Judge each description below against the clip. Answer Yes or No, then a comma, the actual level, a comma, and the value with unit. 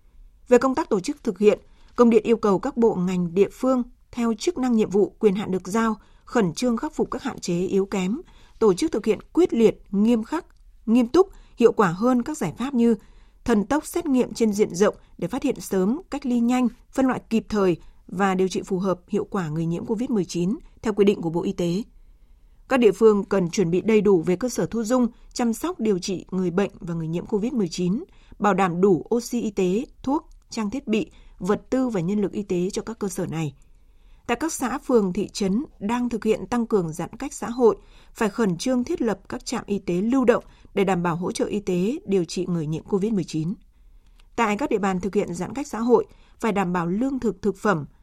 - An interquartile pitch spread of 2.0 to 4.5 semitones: Yes, average, 4.2 semitones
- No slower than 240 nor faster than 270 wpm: No, average, 230 wpm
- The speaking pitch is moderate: No, high, 210 Hz